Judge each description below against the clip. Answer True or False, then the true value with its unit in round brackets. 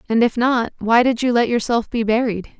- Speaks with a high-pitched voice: True (230 Hz)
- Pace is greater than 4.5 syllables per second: True (5.1 syllables/s)